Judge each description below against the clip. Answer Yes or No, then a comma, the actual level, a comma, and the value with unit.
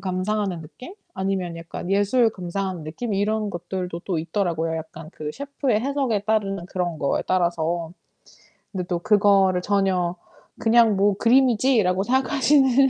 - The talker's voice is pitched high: Yes, high, 195 Hz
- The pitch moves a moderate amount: Yes, average, 4.1 semitones